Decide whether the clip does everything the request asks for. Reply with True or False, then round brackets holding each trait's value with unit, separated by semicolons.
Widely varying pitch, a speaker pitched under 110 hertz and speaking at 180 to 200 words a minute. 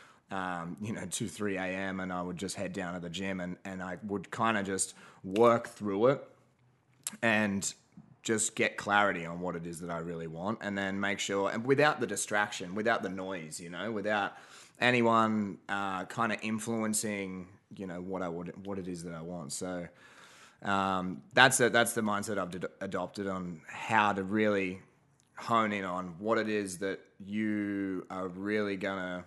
False (2.6 semitones; 100 Hz; 190 wpm)